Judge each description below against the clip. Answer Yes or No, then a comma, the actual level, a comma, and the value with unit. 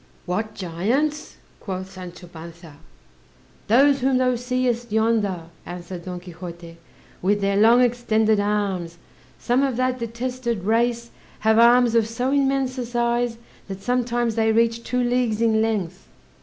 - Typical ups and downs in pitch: Yes, average, 4.4 semitones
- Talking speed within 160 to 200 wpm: No, average, 140 wpm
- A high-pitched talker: Yes, high, 225 Hz